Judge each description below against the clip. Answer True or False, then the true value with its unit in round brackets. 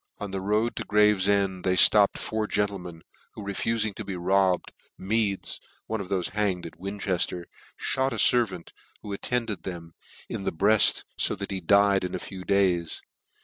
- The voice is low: True (100 Hz)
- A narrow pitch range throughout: True (2.2 semitones)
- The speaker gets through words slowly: False (170 wpm)